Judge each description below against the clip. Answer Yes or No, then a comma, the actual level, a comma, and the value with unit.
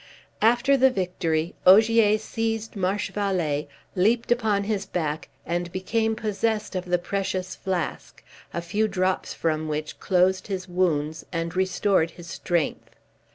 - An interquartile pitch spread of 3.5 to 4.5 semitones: Yes, average, 3.8 semitones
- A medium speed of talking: No, slow, 130 wpm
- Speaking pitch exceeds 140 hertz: Yes, medium, 185 Hz